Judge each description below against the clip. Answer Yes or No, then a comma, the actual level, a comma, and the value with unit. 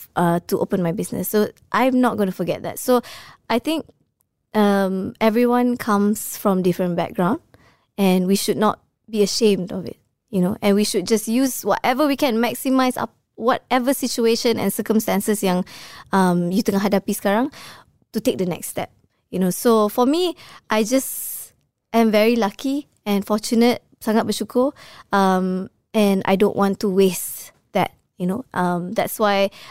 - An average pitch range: Yes, average, 3.6 semitones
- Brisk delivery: Yes, fast, 165 wpm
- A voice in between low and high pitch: No, high, 210 Hz